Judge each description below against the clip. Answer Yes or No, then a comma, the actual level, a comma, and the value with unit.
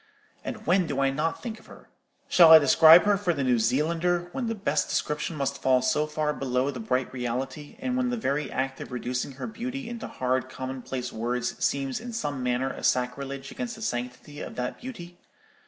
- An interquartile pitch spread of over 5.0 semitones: Yes, wide, 5.5 semitones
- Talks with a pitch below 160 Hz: Yes, medium, 140 Hz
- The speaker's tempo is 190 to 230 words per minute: Yes, fast, 205 wpm